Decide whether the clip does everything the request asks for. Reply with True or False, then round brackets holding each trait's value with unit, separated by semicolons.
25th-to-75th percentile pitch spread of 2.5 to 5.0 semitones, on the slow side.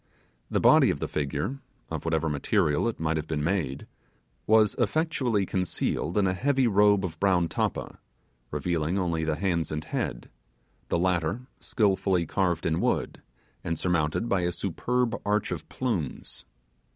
False (4.3 semitones; 150 wpm)